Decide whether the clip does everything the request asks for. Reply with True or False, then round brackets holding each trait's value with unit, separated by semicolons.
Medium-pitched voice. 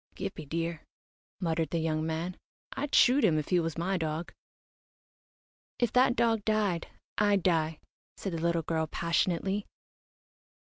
True (170 Hz)